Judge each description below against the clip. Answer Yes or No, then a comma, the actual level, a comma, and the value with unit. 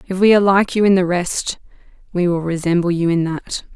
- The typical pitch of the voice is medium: Yes, medium, 180 Hz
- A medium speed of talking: No, fast, 225 wpm